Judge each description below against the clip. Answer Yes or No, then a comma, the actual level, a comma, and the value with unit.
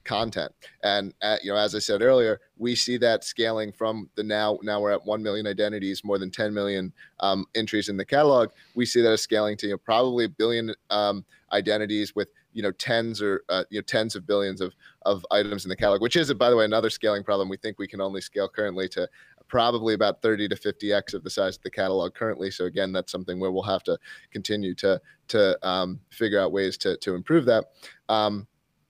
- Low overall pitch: Yes, low, 105 Hz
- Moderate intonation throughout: No, narrow, 2.1 semitones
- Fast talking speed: Yes, fast, 230 wpm